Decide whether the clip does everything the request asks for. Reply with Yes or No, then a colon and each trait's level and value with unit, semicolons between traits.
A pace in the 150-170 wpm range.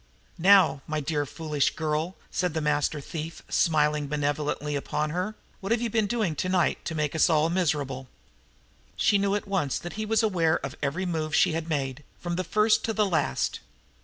No: average, 190 wpm